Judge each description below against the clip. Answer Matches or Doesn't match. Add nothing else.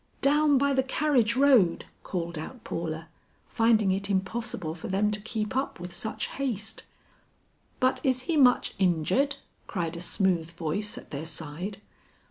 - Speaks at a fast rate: Doesn't match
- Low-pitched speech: Doesn't match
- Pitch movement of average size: Doesn't match